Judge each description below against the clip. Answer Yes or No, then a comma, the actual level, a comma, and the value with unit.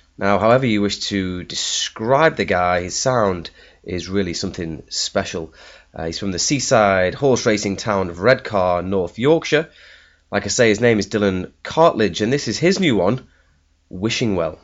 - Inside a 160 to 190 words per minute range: Yes, average, 170 wpm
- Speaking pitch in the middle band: No, low, 100 Hz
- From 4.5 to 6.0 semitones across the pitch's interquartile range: Yes, wide, 5.6 semitones